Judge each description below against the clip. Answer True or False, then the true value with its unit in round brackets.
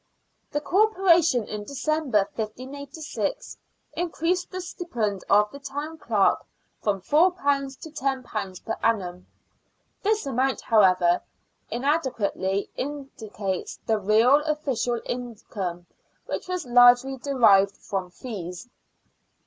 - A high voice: True (250 Hz)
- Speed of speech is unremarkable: False (100 wpm)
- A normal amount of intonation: False (6.3 semitones)